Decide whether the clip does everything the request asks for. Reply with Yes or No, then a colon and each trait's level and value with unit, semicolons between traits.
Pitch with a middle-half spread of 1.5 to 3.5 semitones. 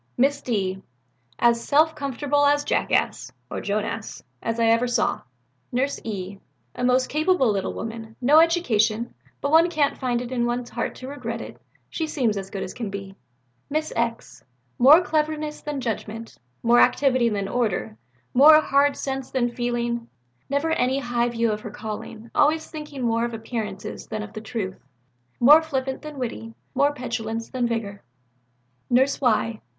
No: average, 4.0 semitones